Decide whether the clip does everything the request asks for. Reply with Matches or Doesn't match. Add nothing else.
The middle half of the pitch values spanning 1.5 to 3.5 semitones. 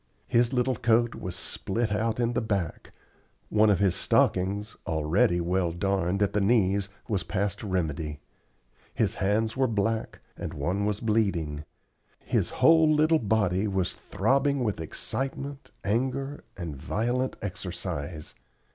Doesn't match